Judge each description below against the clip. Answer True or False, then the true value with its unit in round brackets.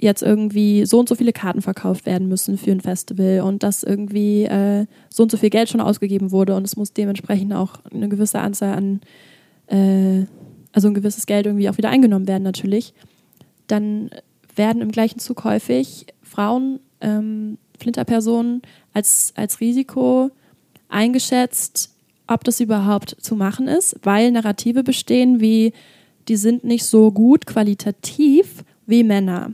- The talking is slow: False (155 wpm)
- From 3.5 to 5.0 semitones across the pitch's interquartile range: False (2.7 semitones)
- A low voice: False (210 Hz)